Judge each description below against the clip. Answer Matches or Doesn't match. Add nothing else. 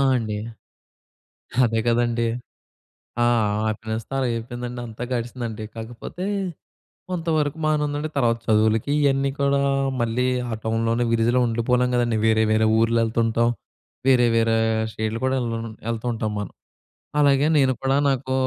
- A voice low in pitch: Matches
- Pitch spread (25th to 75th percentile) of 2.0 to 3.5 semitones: Matches